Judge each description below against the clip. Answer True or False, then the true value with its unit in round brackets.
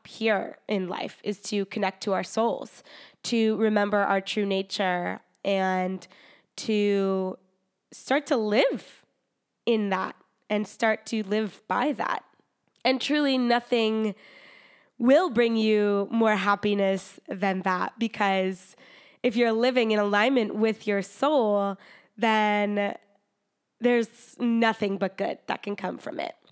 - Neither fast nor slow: False (125 wpm)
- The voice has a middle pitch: False (210 Hz)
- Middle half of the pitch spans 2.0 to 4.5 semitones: True (2.8 semitones)